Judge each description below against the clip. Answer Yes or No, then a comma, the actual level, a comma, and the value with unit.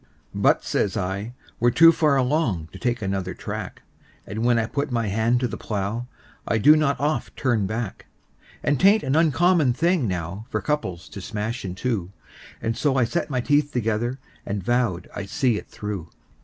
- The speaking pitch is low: Yes, low, 120 Hz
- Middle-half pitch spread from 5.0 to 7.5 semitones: Yes, wide, 5.6 semitones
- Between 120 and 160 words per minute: No, average, 185 wpm